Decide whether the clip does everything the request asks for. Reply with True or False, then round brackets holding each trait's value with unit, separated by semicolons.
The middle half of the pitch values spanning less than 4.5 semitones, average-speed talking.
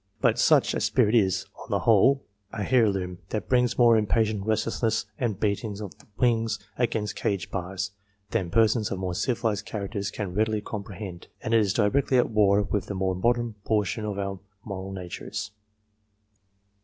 True (2.6 semitones; 165 wpm)